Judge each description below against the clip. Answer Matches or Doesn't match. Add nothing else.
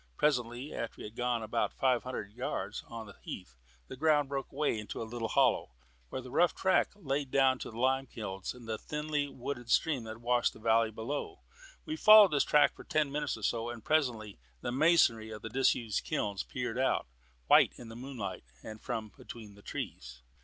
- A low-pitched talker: Matches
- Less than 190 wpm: Doesn't match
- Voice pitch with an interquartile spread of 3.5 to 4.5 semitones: Matches